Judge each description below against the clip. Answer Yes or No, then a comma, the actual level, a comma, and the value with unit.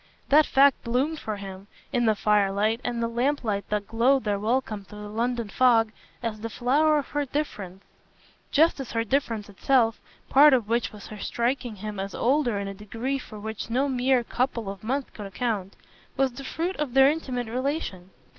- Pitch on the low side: No, high, 235 Hz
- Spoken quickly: No, average, 185 wpm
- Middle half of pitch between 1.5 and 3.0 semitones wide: No, average, 4.2 semitones